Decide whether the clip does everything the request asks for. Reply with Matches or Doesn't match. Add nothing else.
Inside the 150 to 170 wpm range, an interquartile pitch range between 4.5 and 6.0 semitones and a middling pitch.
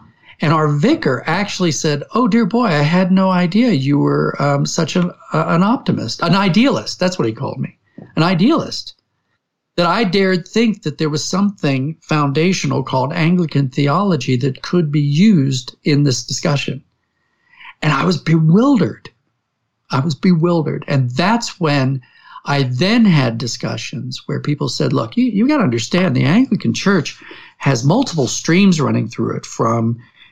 Matches